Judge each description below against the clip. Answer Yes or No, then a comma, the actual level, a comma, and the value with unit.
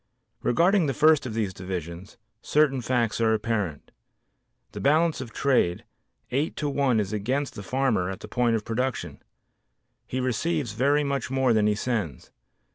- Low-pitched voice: Yes, low, 125 Hz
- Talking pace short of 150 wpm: No, average, 160 wpm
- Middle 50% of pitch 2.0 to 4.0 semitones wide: No, average, 4.8 semitones